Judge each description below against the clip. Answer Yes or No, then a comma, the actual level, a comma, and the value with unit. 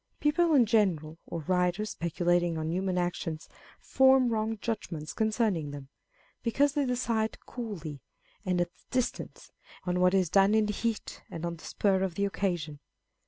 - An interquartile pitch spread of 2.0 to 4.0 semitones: No, average, 4.7 semitones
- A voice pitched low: No, high, 190 Hz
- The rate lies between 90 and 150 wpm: No, average, 160 wpm